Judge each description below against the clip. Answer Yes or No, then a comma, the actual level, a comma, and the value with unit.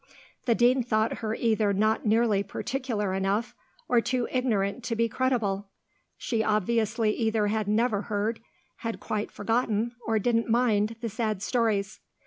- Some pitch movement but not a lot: No, narrow, 2.1 semitones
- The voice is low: No, high, 220 Hz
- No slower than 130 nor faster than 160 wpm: Yes, average, 145 wpm